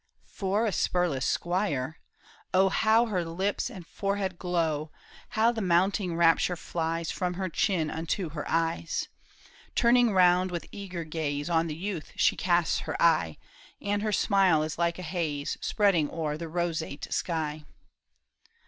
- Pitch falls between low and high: Yes, medium, 175 Hz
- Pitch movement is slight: No, average, 3.1 semitones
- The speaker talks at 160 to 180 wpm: No, average, 150 wpm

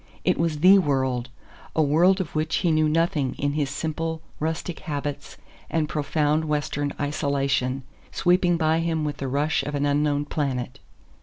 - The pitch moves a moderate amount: No, narrow, 2.2 semitones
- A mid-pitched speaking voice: Yes, medium, 150 Hz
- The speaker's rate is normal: Yes, average, 160 wpm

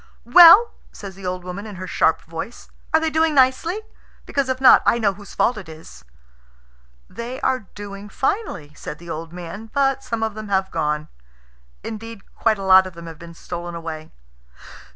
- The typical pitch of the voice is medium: No, high, 200 Hz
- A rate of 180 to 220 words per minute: Yes, average, 185 wpm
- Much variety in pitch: Yes, wide, 6.9 semitones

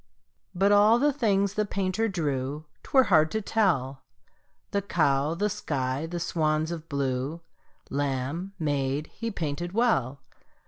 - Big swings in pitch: Yes, wide, 6.2 semitones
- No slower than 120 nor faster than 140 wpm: Yes, slow, 135 wpm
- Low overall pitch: No, medium, 165 Hz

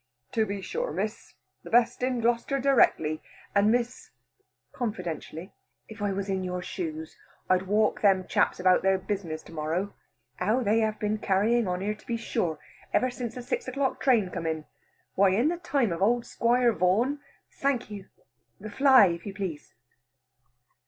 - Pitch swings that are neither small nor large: Yes, average, 4.6 semitones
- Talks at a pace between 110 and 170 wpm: No, average, 180 wpm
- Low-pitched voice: No, high, 205 Hz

